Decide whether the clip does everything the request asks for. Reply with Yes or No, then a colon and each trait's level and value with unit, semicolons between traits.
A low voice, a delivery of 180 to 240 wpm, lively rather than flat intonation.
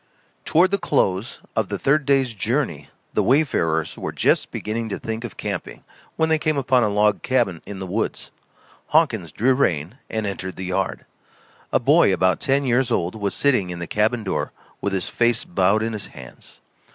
Yes: low, 110 Hz; average, 190 wpm; wide, 5.7 semitones